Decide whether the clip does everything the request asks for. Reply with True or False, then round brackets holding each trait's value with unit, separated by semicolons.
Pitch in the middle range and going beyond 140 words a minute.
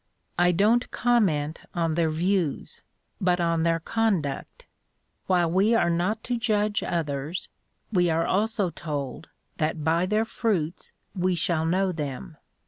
False (175 Hz; 135 wpm)